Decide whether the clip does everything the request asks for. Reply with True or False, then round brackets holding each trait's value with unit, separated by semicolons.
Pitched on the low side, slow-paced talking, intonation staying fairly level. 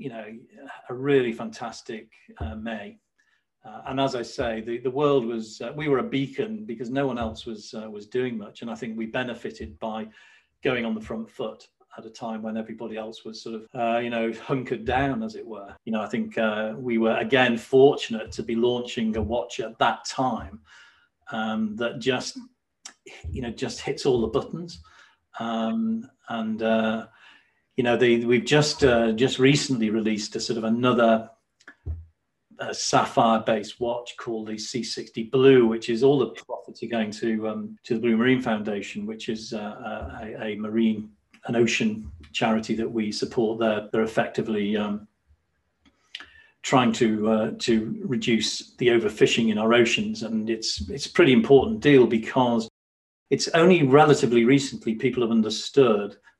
False (115 Hz; 175 wpm; 2.3 semitones)